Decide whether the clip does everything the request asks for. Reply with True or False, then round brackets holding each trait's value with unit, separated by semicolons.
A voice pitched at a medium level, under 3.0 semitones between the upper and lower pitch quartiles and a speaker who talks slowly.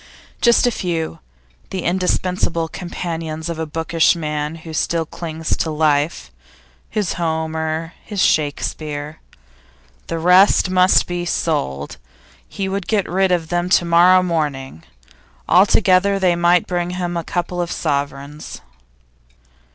True (170 Hz; 2.5 semitones; 130 wpm)